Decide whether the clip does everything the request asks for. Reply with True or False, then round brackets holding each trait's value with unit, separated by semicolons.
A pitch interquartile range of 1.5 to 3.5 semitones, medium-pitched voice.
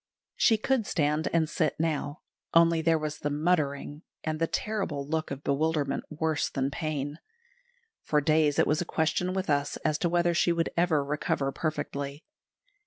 True (2.4 semitones; 155 Hz)